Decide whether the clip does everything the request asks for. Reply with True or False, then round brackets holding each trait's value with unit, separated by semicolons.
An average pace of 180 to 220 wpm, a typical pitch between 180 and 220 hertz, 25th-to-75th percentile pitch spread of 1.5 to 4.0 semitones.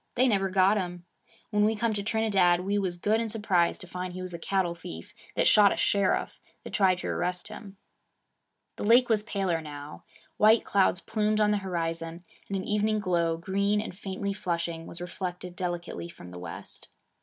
True (190 wpm; 190 Hz; 3.1 semitones)